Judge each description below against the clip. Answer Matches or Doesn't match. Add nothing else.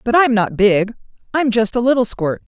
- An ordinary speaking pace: Doesn't match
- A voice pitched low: Doesn't match